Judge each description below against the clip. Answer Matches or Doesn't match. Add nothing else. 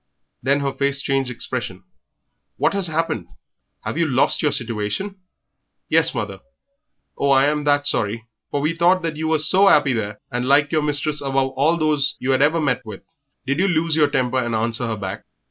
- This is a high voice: Doesn't match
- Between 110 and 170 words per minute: Doesn't match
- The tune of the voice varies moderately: Matches